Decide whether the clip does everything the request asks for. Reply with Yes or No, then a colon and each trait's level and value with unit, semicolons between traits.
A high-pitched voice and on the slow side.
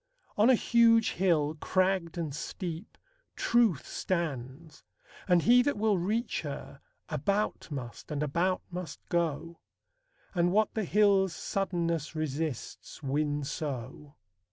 No: medium, 170 Hz; slow, 120 wpm